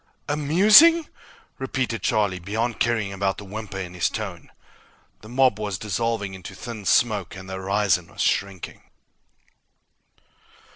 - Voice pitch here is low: Yes, low, 105 Hz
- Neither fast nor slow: No, slow, 130 wpm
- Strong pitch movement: No, average, 3.8 semitones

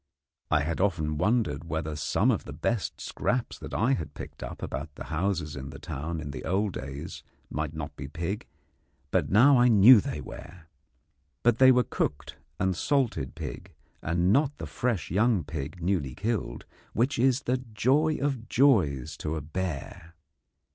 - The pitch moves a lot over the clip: Yes, wide, 7.8 semitones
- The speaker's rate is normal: Yes, average, 175 wpm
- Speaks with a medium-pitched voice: No, very low, 95 Hz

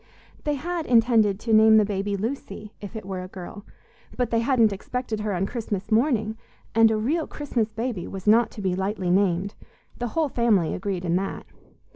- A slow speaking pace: No, average, 190 wpm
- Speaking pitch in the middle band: No, high, 215 Hz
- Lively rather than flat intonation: No, average, 3.3 semitones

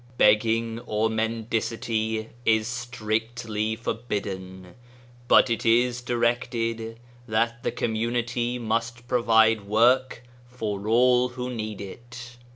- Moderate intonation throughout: No, narrow, 1.6 semitones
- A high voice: No, low, 115 Hz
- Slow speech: Yes, slow, 105 wpm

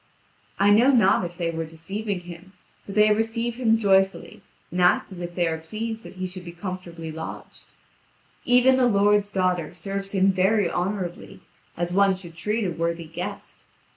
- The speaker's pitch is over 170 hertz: Yes, high, 190 Hz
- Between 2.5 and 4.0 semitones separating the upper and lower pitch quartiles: Yes, average, 3.3 semitones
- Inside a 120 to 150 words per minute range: No, average, 175 wpm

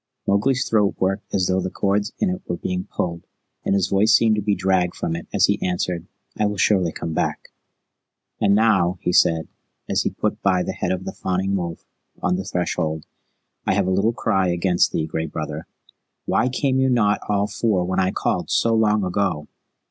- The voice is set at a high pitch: No, very low, 95 Hz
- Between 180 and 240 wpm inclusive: Yes, average, 200 wpm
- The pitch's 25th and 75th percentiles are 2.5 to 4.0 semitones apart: Yes, average, 2.8 semitones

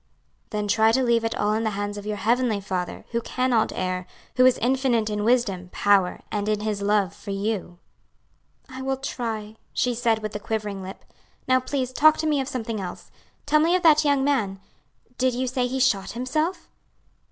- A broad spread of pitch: No, average, 3.9 semitones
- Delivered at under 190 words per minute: No, average, 200 wpm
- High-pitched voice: Yes, high, 225 Hz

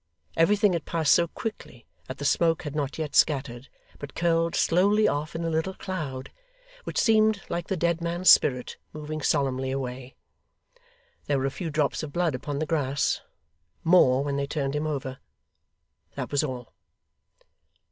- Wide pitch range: No, average, 3.8 semitones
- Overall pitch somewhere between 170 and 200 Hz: No, medium, 150 Hz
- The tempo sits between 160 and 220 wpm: Yes, average, 165 wpm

